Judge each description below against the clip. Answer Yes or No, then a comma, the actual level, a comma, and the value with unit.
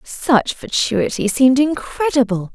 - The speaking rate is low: Yes, slow, 95 wpm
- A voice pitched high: Yes, very high, 255 Hz